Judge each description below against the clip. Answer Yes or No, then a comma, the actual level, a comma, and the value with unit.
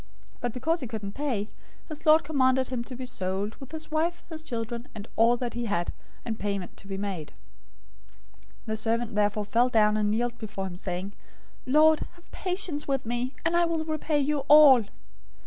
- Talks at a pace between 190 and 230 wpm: Yes, average, 200 wpm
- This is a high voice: Yes, high, 240 Hz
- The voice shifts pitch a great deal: Yes, wide, 6.1 semitones